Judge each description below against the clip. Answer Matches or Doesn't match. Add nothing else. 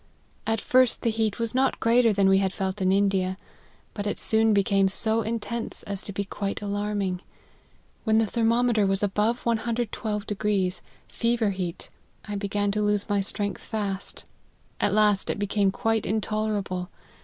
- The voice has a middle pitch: Doesn't match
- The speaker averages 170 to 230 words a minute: Doesn't match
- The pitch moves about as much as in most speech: Doesn't match